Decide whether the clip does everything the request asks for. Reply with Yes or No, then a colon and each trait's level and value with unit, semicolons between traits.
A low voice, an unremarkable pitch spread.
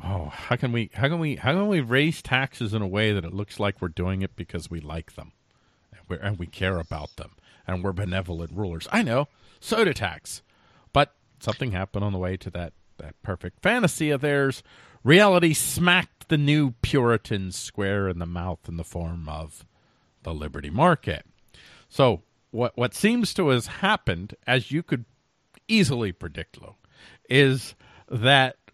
No: low, 110 Hz; wide, 6.9 semitones